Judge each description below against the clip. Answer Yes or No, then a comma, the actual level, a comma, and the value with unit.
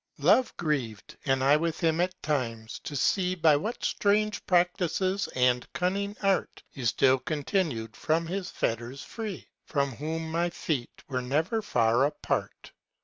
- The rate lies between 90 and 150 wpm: Yes, average, 145 wpm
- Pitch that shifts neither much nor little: No, wide, 5.9 semitones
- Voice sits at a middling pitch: Yes, medium, 155 Hz